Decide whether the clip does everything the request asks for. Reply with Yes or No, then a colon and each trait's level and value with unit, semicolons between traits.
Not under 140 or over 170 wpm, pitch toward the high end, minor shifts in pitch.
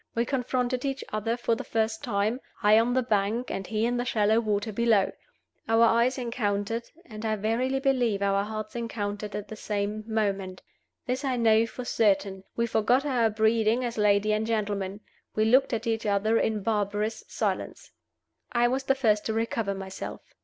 No: average, 180 wpm; high, 220 Hz; narrow, 2.3 semitones